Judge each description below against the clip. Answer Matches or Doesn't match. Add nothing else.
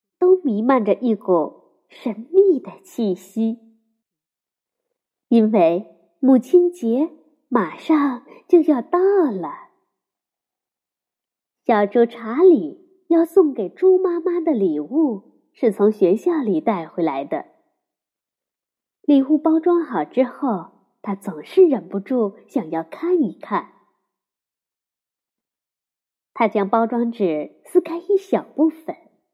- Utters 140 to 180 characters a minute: Matches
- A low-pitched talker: Doesn't match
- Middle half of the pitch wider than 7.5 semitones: Matches